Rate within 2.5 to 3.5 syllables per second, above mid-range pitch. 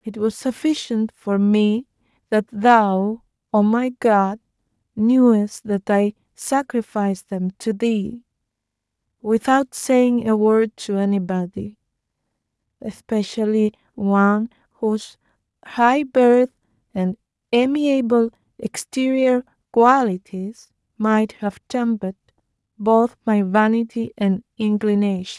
Yes: 3.3 syllables/s; high, 220 Hz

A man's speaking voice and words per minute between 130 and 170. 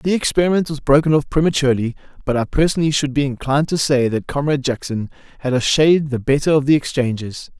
No: male; average, 195 wpm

